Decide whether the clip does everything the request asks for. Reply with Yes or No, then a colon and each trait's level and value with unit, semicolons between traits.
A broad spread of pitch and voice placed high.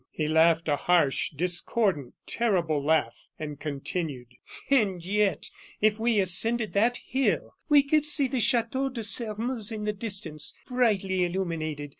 Yes: wide, 6.4 semitones; high, 195 Hz